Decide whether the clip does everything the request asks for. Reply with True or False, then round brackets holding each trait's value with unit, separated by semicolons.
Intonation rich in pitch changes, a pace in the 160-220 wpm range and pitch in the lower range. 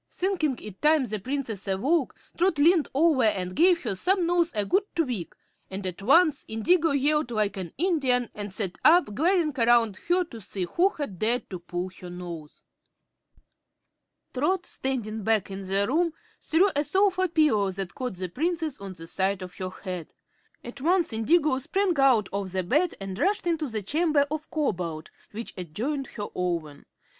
False (8.9 semitones; 170 wpm; 250 Hz)